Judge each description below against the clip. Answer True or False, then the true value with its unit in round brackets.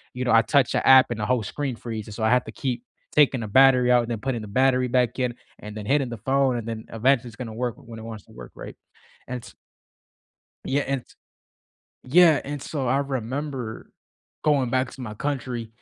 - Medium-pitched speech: False (125 Hz)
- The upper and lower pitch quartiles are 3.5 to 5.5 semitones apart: False (2.8 semitones)